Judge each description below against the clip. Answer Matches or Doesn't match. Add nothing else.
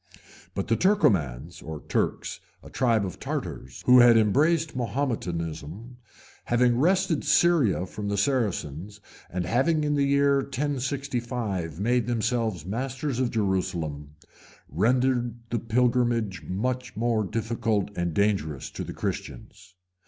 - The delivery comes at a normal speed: Doesn't match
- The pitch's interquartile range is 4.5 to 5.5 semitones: Matches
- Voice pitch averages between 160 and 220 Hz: Doesn't match